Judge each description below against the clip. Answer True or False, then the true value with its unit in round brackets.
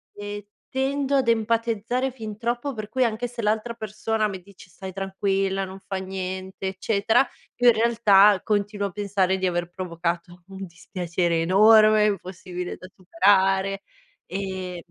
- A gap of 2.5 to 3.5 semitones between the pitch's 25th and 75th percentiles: True (2.8 semitones)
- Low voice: False (200 Hz)